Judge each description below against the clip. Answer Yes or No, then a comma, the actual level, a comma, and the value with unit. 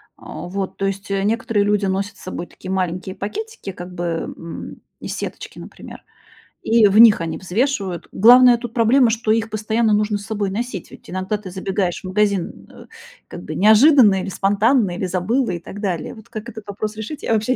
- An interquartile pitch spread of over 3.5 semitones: No, average, 3.1 semitones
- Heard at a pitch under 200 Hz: No, high, 205 Hz